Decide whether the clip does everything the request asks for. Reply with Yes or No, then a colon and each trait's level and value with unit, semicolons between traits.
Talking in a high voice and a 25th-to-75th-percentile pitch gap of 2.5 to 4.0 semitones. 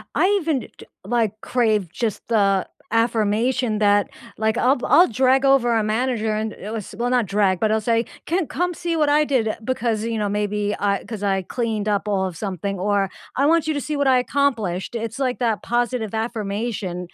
Yes: high, 225 Hz; average, 3.6 semitones